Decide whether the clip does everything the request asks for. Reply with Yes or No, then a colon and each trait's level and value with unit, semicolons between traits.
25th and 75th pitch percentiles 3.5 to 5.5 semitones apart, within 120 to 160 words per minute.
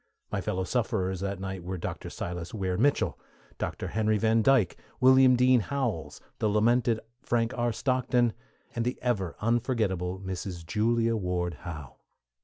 Yes: average, 4.5 semitones; average, 145 wpm